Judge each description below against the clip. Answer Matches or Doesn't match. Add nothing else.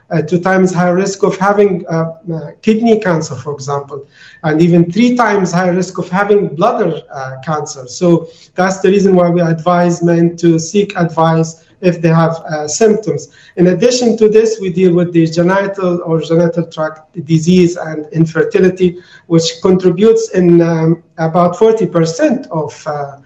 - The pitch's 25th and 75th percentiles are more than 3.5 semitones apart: Doesn't match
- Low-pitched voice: Doesn't match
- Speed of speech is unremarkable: Matches